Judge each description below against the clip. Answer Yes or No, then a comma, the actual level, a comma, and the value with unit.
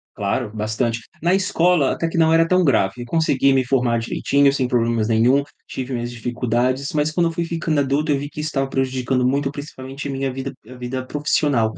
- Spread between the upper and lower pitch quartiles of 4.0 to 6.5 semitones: No, average, 3.5 semitones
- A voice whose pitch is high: No, low, 135 Hz